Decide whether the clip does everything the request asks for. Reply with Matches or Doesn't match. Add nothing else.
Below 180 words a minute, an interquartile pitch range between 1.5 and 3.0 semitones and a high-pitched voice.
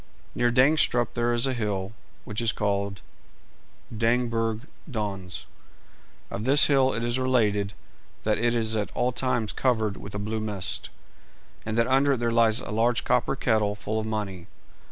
Doesn't match